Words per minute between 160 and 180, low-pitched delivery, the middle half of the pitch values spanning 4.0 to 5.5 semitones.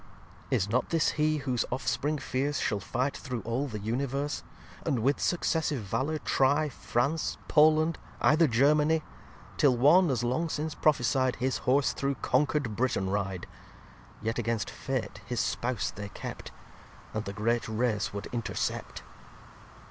No: average, 145 wpm; low, 130 Hz; average, 4.3 semitones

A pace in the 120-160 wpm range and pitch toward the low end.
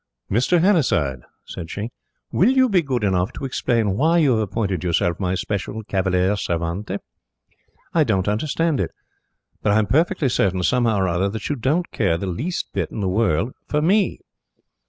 No: average, 180 wpm; low, 105 Hz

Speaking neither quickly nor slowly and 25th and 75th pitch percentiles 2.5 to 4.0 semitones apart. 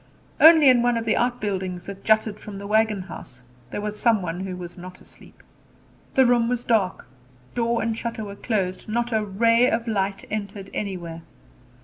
Yes: average, 180 wpm; average, 3.4 semitones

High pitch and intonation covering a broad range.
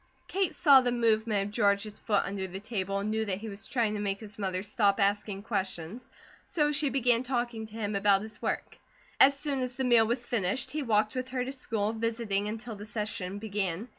No: high, 220 Hz; average, 3.4 semitones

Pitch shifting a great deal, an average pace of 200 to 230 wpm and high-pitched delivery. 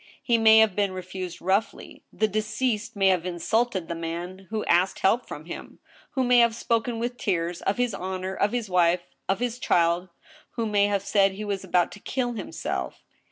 No: average, 3.8 semitones; fast, 205 wpm; high, 200 Hz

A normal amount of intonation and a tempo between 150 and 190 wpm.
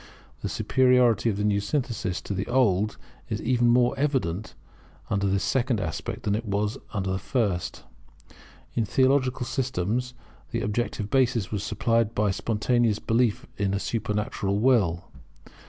No: average, 3.7 semitones; average, 140 wpm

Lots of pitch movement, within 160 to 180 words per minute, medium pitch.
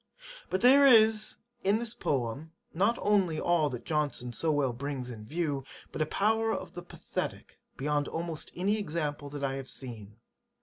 Yes: wide, 6.7 semitones; average, 170 wpm; medium, 155 Hz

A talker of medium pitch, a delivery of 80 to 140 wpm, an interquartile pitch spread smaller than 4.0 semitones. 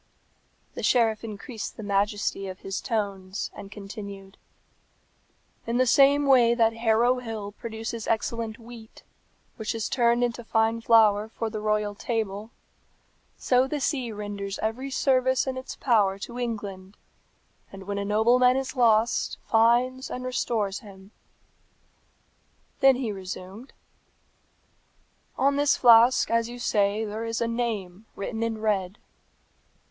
No: high, 225 Hz; slow, 135 wpm; average, 2.9 semitones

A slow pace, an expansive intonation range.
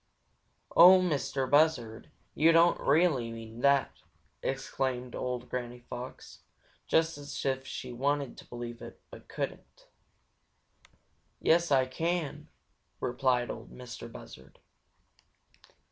No: slow, 110 wpm; average, 3.9 semitones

